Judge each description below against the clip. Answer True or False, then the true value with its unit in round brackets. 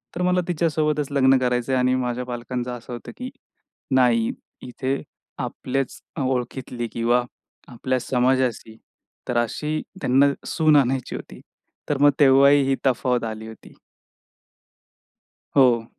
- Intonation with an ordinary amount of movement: False (2.2 semitones)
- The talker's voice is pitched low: True (130 Hz)